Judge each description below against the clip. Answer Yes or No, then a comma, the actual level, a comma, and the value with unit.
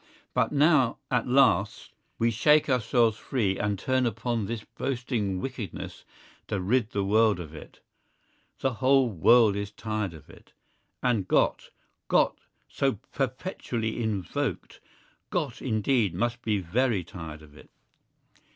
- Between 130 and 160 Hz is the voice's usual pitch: No, low, 115 Hz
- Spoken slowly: Yes, slow, 125 wpm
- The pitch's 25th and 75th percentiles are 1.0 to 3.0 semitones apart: No, average, 4.3 semitones